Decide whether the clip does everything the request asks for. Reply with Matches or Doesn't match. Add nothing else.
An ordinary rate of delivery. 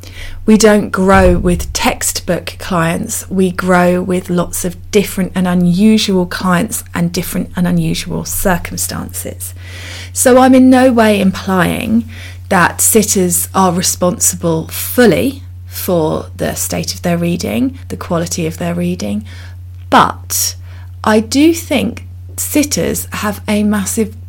Doesn't match